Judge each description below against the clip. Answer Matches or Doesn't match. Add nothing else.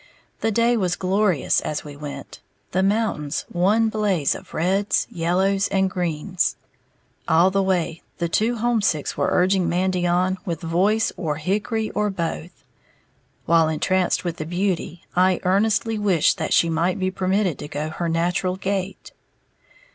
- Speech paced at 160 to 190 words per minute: Doesn't match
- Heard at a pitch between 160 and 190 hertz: Matches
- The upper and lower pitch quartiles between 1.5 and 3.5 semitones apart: Matches